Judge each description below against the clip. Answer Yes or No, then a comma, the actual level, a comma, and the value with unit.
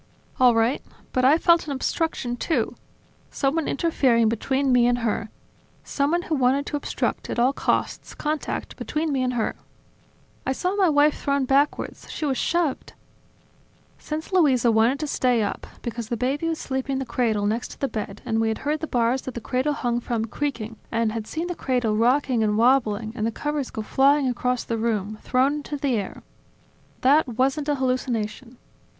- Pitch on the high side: Yes, very high, 255 Hz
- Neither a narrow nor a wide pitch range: Yes, average, 3.9 semitones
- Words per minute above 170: Yes, average, 185 wpm